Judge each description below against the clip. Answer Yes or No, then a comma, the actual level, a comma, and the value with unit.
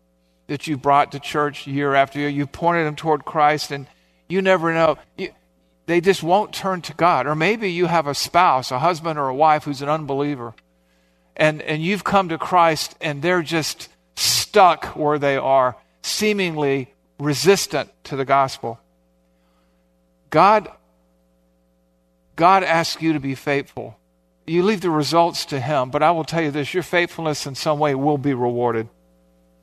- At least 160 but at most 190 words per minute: Yes, average, 170 wpm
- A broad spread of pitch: Yes, wide, 7.2 semitones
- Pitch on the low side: No, medium, 145 Hz